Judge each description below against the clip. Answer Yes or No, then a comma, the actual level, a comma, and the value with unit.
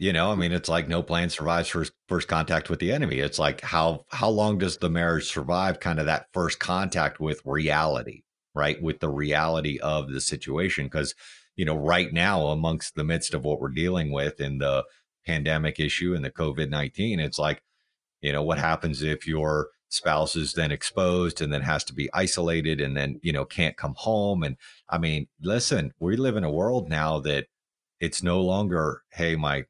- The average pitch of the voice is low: Yes, very low, 80 Hz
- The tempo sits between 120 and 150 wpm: No, average, 200 wpm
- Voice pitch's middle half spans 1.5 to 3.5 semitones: Yes, narrow, 2.4 semitones